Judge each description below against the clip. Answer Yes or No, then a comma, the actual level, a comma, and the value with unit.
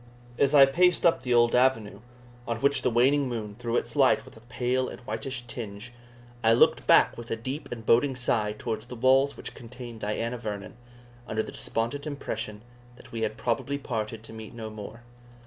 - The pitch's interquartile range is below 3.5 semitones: Yes, average, 2.8 semitones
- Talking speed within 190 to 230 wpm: Yes, average, 195 wpm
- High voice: No, low, 120 Hz